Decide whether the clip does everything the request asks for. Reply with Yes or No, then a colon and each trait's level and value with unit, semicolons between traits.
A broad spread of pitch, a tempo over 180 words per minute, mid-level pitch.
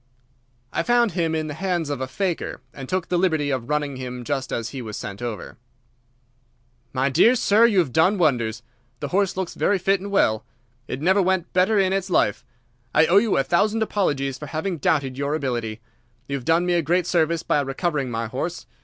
Yes: wide, 5.9 semitones; fast, 205 wpm; medium, 160 Hz